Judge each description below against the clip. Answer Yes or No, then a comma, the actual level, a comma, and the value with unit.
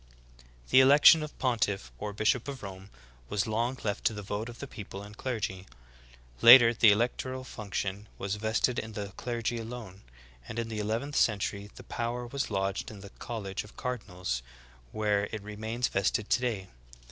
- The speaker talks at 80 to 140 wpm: No, average, 170 wpm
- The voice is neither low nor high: No, low, 110 Hz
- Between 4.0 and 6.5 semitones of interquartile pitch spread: No, average, 3.1 semitones